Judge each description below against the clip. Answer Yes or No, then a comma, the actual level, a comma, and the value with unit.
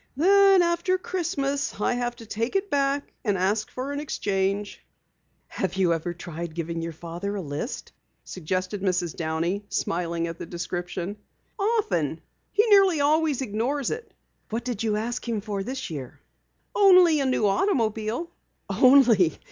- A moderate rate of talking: Yes, average, 150 wpm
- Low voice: No, high, 215 Hz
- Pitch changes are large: Yes, wide, 8.2 semitones